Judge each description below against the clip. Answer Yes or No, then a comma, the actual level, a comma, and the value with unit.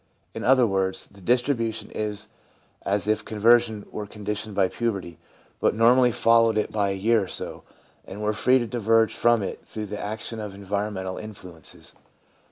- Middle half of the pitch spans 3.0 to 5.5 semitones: No, narrow, 2.4 semitones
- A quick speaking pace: No, average, 175 wpm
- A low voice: Yes, low, 105 Hz